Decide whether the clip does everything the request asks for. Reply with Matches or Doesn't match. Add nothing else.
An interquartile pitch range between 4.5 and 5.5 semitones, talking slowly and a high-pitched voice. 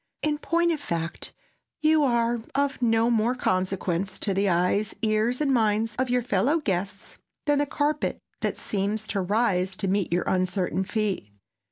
Doesn't match